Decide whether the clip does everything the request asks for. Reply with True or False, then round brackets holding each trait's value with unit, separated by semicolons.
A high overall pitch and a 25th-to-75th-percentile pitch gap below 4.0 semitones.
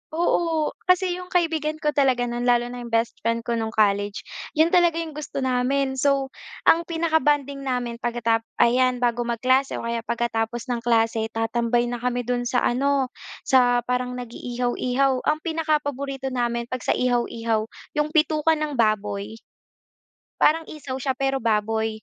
True (250 Hz; 3.4 semitones)